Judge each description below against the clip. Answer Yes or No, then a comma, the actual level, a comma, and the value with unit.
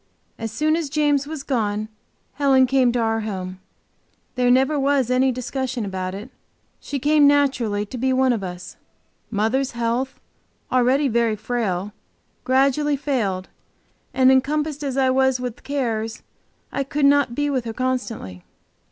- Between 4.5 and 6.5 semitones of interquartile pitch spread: No, average, 3.7 semitones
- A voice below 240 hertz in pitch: No, very high, 255 Hz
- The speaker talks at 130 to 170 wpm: Yes, average, 150 wpm